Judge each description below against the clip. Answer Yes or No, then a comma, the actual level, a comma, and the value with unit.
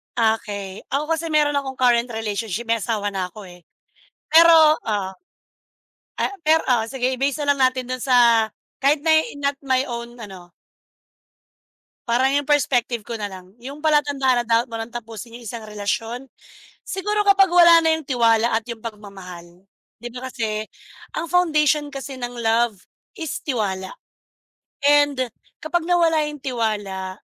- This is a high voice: Yes, high, 245 Hz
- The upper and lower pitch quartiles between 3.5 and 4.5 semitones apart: No, average, 4.9 semitones